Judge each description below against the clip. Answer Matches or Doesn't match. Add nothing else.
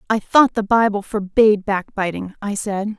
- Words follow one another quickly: Doesn't match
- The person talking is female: Matches